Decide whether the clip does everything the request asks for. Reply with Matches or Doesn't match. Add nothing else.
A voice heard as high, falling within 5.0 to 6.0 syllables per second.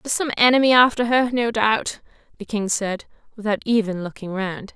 Matches